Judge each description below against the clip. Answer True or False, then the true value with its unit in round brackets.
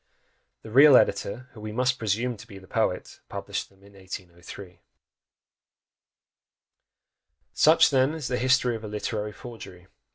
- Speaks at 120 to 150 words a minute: True (140 wpm)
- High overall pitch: False (110 Hz)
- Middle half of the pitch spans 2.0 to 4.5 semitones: True (4.2 semitones)